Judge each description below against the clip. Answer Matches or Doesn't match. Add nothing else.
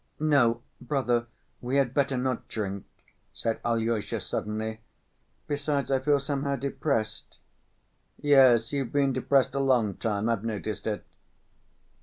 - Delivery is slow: Matches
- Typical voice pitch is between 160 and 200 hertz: Doesn't match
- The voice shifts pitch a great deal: Doesn't match